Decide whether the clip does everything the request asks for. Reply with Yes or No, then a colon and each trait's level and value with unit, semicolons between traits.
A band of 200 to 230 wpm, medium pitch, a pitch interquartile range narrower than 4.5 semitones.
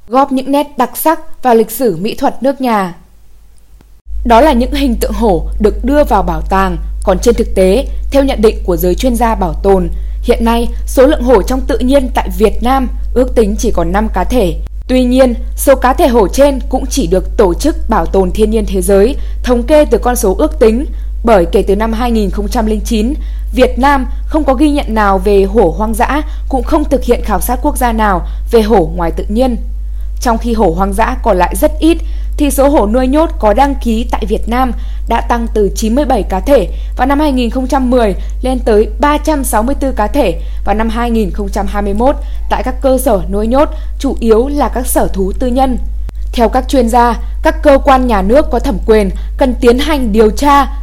No: average, 210 wpm; high, 240 Hz; average, 4.1 semitones